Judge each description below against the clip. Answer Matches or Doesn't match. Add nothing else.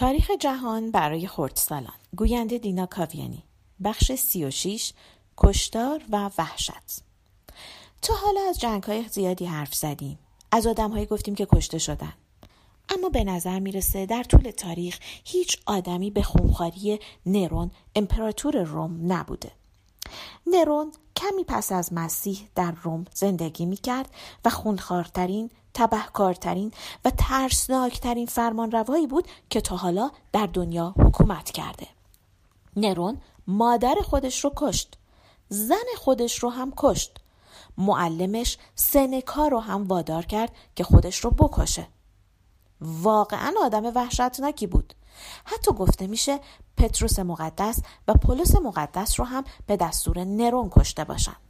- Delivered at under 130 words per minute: Matches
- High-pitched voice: Matches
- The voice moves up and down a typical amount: Doesn't match